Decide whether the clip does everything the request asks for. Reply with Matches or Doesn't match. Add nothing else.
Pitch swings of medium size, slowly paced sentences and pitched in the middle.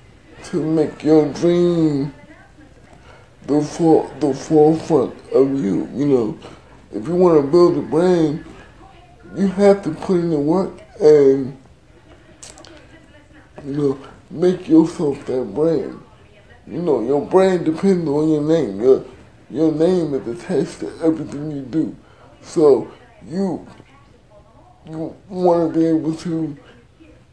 Matches